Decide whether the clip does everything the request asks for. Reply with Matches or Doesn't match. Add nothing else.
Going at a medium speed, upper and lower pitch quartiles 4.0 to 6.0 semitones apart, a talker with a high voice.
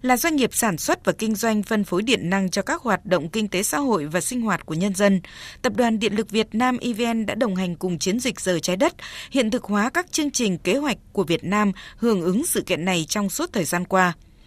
Doesn't match